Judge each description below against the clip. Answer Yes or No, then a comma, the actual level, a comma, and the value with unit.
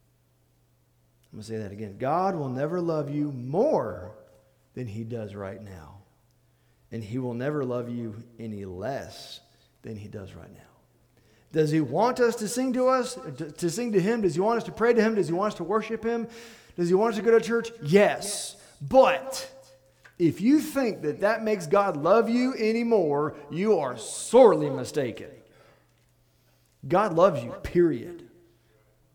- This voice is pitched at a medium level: Yes, medium, 150 Hz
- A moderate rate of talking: Yes, average, 175 wpm